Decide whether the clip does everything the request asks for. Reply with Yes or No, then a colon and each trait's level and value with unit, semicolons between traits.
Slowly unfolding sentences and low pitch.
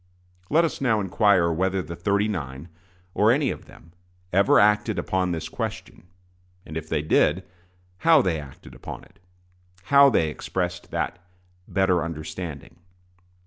No: average, 145 wpm; very low, 90 Hz